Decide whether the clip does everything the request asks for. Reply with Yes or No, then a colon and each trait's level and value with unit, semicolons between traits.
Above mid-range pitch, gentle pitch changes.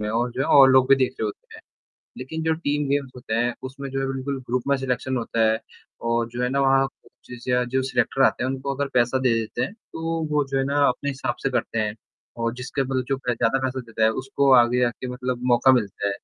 No: low, 130 Hz; narrow, 2.1 semitones